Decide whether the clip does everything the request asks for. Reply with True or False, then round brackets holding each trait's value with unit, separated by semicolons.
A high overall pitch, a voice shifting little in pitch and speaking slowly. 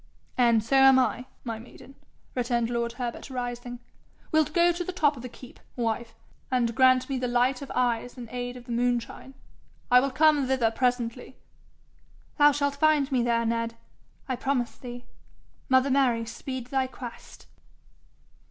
False (250 Hz; 2.0 semitones; 160 wpm)